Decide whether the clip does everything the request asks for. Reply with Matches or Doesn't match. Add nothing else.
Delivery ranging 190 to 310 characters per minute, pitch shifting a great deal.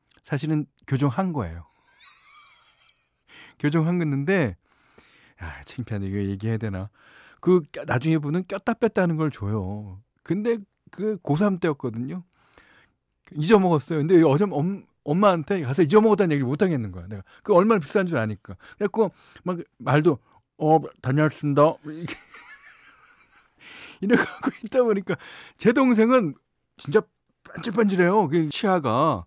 Matches